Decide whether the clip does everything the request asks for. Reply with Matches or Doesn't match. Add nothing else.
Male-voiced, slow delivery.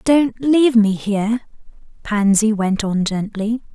Doesn't match